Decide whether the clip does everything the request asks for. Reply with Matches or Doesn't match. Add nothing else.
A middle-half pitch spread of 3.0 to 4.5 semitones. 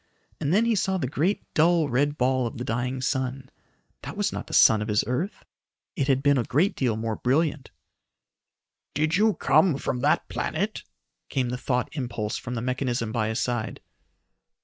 Matches